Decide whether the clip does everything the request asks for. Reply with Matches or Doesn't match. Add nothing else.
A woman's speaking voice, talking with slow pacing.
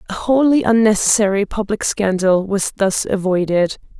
Matches